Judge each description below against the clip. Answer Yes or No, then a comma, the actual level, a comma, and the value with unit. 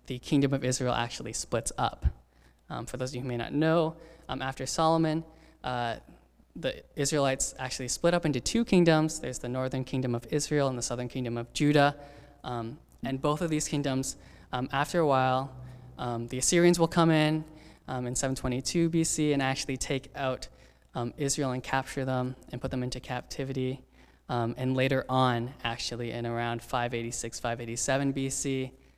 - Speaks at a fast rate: No, average, 175 wpm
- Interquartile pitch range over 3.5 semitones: No, average, 2.9 semitones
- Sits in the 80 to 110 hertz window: No, low, 130 Hz